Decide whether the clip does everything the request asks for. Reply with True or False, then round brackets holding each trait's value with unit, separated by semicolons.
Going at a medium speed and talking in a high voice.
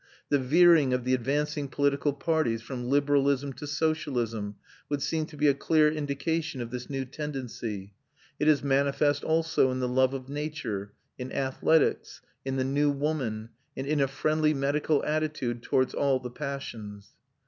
False (160 wpm; 140 Hz)